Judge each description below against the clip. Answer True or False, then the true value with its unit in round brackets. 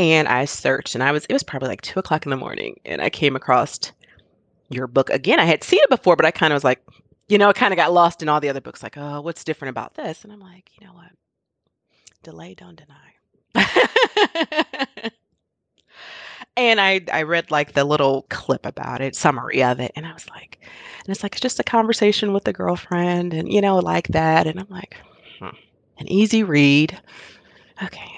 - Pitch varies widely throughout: True (6.3 semitones)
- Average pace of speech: False (210 wpm)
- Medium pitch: True (165 Hz)